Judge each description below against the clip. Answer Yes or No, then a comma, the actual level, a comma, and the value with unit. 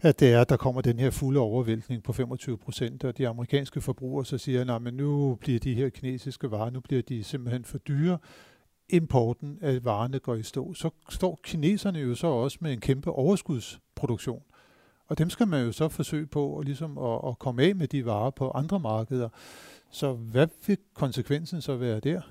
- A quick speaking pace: No, average, 200 wpm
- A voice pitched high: No, low, 135 Hz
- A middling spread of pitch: Yes, average, 3.3 semitones